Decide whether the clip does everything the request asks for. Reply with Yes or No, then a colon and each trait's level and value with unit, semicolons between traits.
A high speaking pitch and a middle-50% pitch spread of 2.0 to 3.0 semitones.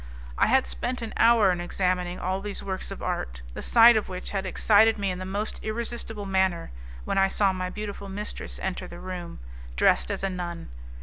Yes: high, 195 Hz; average, 2.7 semitones